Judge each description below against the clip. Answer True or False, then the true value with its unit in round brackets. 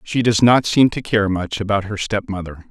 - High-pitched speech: False (105 Hz)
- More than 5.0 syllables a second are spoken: True (5.2 syllables/s)